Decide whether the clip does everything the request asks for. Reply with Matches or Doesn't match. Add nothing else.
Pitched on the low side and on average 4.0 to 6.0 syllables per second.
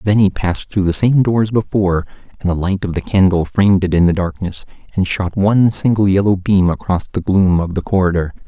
Matches